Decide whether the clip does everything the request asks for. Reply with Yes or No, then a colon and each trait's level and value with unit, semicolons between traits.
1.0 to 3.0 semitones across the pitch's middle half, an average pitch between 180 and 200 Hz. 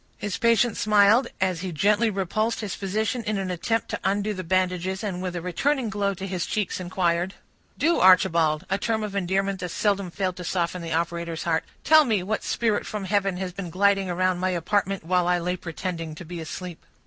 Yes: narrow, 2.6 semitones; high, 190 Hz